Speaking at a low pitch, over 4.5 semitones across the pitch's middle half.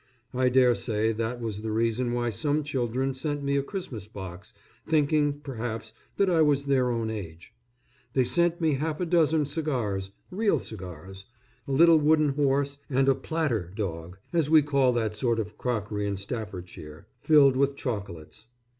Yes: low, 125 Hz; average, 5.3 semitones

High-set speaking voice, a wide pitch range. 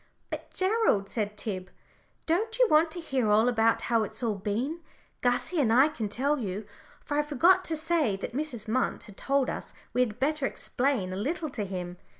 Yes: very high, 250 Hz; wide, 6.5 semitones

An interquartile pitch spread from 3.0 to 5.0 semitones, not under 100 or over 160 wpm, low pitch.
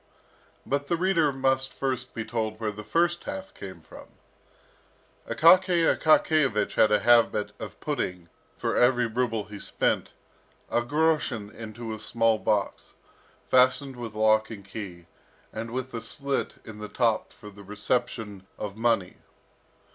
Yes: average, 3.9 semitones; average, 145 wpm; low, 115 Hz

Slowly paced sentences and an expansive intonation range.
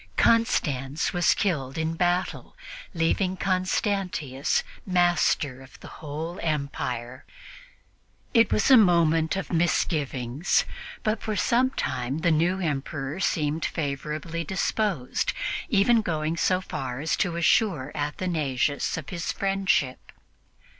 No: slow, 115 wpm; average, 4.6 semitones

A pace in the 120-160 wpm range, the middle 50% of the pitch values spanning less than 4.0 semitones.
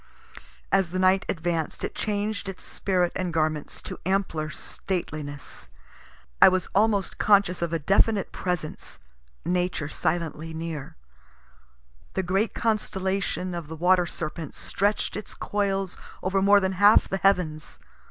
Yes: slow, 135 wpm; average, 3.0 semitones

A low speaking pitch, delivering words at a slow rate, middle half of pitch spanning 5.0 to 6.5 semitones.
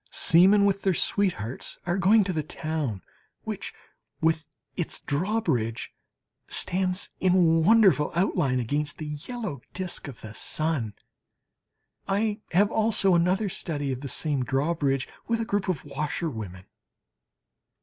No: medium, 165 Hz; slow, 130 wpm; wide, 5.5 semitones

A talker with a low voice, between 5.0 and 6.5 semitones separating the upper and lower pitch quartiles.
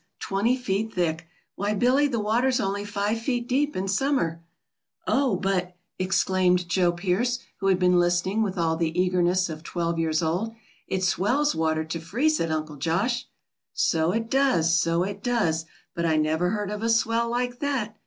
No: high, 190 Hz; average, 5.3 semitones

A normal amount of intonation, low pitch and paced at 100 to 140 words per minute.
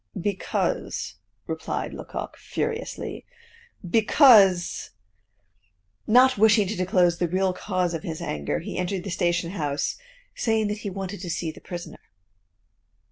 No: average, 3.7 semitones; medium, 185 Hz; slow, 135 wpm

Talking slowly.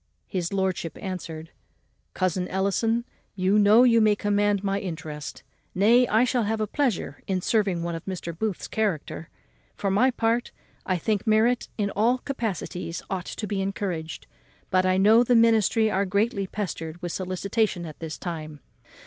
No: average, 160 wpm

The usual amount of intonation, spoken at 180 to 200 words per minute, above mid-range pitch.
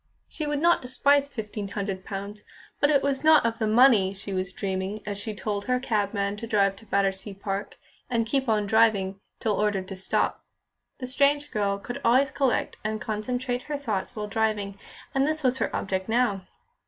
Yes: average, 4.2 semitones; average, 190 wpm; high, 215 Hz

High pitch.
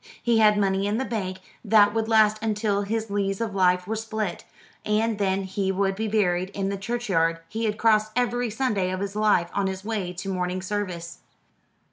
Yes: high, 205 Hz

